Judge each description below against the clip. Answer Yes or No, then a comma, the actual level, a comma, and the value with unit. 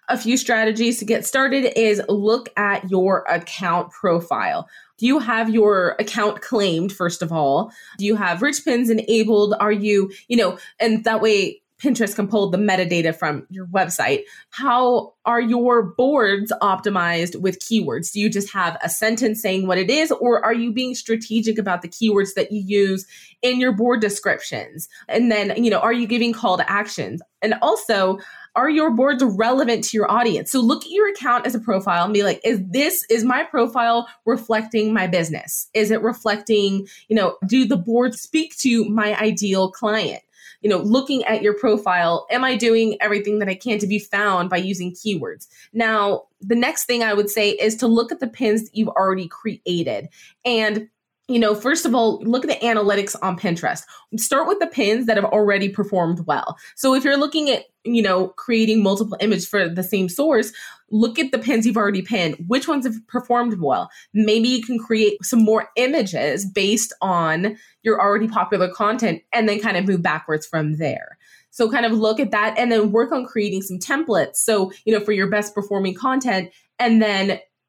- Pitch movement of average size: Yes, average, 3.3 semitones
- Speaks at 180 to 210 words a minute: Yes, average, 195 wpm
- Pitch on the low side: No, high, 220 Hz